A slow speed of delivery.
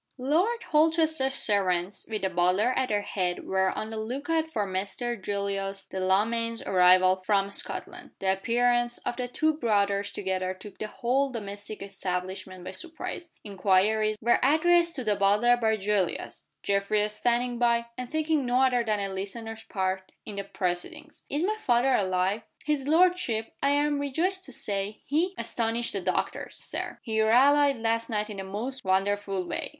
No: average, 165 wpm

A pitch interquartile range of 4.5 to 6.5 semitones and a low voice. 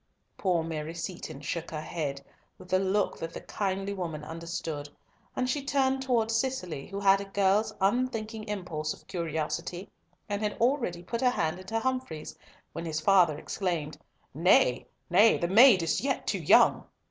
No: average, 5.1 semitones; medium, 185 Hz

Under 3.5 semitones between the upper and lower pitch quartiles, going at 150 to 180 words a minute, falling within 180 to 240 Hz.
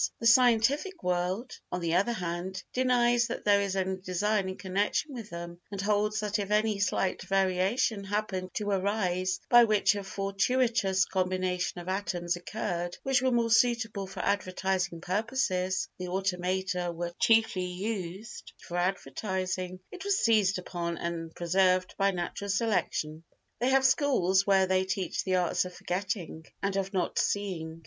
Yes: average, 2.8 semitones; average, 155 wpm; high, 190 Hz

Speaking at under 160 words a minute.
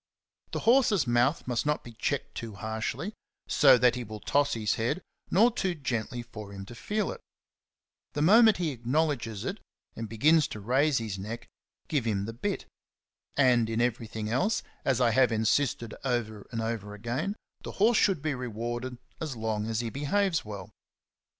No: average, 175 wpm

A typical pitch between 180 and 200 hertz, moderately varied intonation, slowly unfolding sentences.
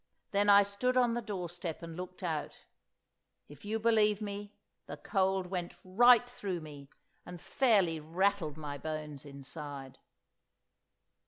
Yes: medium, 185 Hz; average, 4.9 semitones; slow, 130 wpm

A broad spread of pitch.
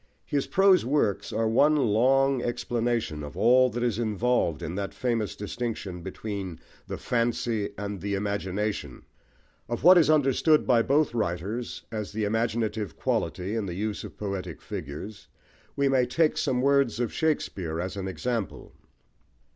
No: average, 4.1 semitones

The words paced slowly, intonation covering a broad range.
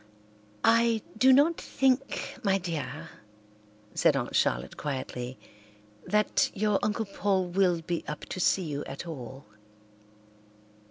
Yes: slow, 120 wpm; wide, 6.2 semitones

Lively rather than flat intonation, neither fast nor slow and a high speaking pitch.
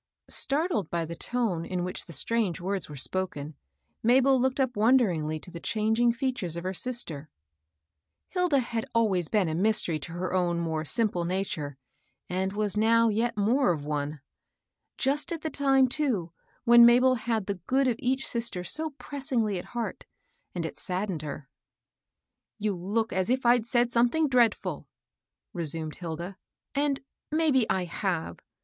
Yes: wide, 6.2 semitones; average, 165 wpm; high, 215 Hz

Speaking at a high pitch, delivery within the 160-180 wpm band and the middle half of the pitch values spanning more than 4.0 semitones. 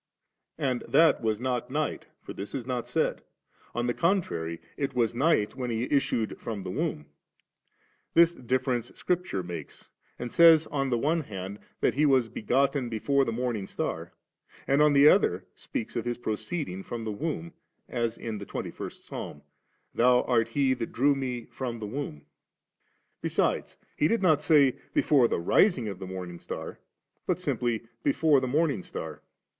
No: low, 125 Hz; average, 175 wpm; average, 4.6 semitones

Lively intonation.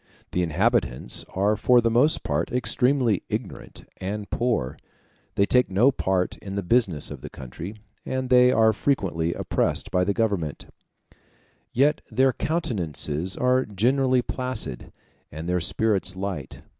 Yes: wide, 5.8 semitones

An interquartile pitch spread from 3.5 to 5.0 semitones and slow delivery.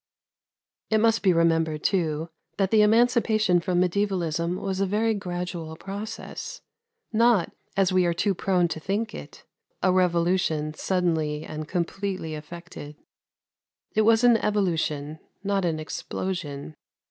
Yes: average, 3.9 semitones; slow, 130 wpm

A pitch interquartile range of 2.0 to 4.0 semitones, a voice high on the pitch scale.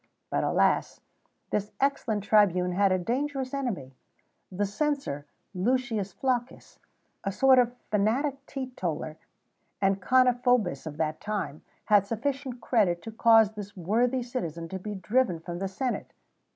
No: average, 5.3 semitones; high, 215 Hz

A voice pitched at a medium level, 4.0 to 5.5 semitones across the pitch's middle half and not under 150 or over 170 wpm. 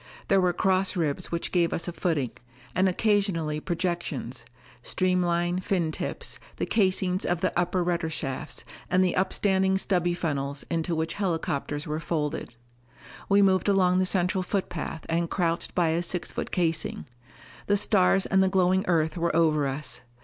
No: medium, 175 Hz; narrow, 2.5 semitones; average, 160 wpm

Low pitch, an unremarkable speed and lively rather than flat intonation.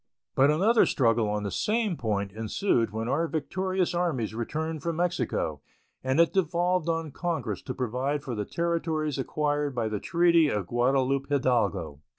No: medium, 145 Hz; average, 160 wpm; wide, 6.2 semitones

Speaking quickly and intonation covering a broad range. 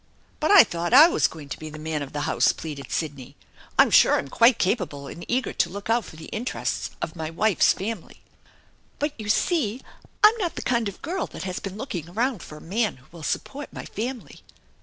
Yes: fast, 225 wpm; wide, 7.6 semitones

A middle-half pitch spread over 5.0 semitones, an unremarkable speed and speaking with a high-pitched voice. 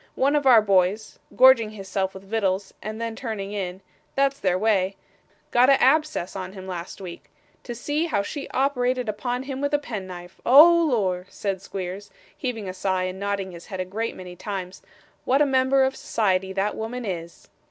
Yes: wide, 5.4 semitones; average, 195 wpm; high, 210 Hz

